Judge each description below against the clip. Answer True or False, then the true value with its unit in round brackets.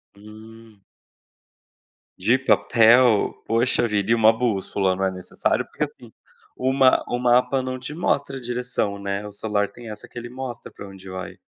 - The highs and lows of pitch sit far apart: False (3.6 semitones)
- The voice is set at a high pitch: False (115 Hz)